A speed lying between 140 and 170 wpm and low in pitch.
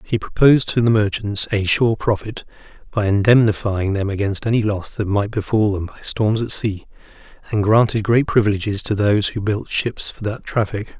No: average, 185 wpm; low, 105 Hz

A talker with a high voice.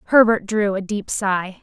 Yes: high, 205 Hz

